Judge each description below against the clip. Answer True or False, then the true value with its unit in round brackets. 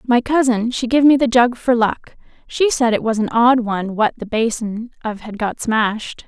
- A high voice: True (235 Hz)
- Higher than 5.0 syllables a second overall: False (4.8 syllables/s)